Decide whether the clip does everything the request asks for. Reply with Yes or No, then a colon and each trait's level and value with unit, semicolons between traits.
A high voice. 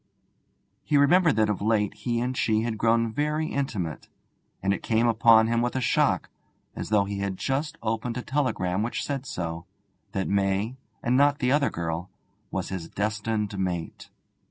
No: low, 110 Hz